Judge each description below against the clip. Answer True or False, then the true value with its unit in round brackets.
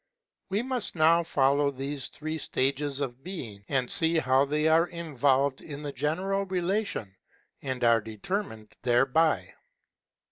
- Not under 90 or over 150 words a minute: True (135 wpm)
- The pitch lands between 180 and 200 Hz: False (145 Hz)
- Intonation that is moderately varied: True (4.4 semitones)